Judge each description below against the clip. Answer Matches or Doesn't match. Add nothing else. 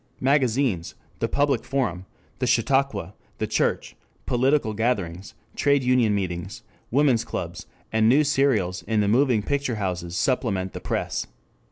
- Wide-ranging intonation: Matches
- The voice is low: Matches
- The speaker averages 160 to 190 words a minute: Doesn't match